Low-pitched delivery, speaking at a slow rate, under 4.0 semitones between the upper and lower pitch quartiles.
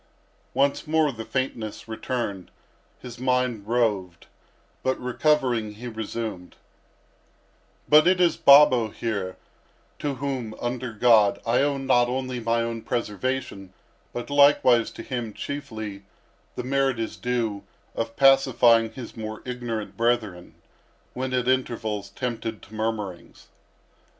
Yes: low, 120 Hz; slow, 115 wpm; average, 2.9 semitones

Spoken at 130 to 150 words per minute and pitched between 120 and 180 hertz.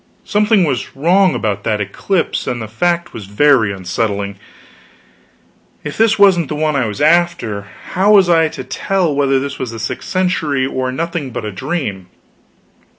No: average, 165 wpm; medium, 140 Hz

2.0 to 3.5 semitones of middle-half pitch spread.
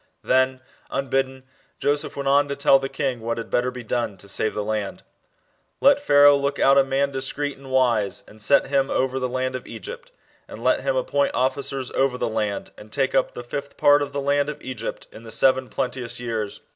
Yes: narrow, 2.5 semitones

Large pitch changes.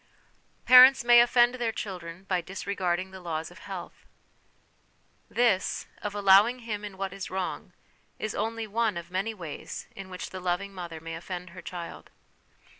No: average, 3.6 semitones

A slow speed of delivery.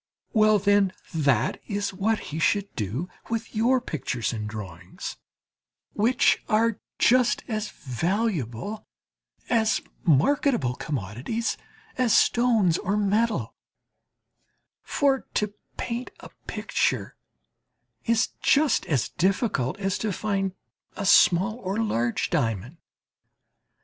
Yes: slow, 105 wpm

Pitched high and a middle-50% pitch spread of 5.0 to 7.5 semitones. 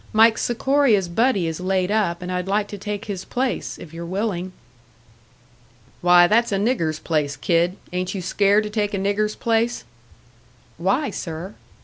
No: high, 195 Hz; average, 3.5 semitones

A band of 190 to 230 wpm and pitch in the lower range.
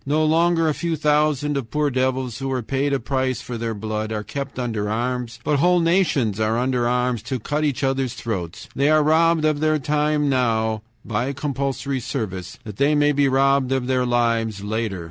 Yes: average, 200 wpm; low, 130 Hz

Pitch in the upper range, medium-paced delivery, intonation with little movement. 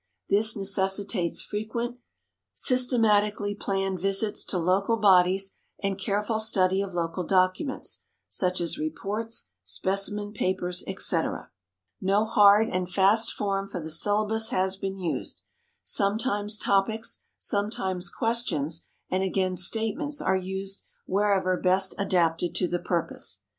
No: high, 195 Hz; slow, 120 wpm; narrow, 2.3 semitones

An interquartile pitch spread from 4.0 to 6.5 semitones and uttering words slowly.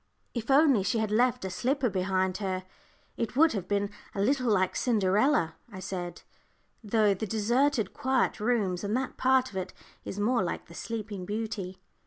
No: average, 4.6 semitones; average, 175 wpm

